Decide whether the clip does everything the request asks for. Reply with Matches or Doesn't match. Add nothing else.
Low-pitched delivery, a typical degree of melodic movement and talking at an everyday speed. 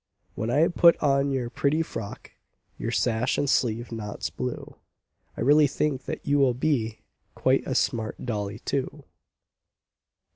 Matches